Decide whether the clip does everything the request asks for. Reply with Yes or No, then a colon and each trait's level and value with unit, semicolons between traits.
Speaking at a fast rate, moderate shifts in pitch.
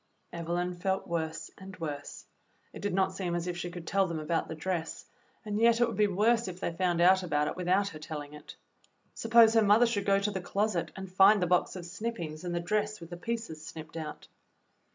Yes: fast, 230 wpm; average, 3.4 semitones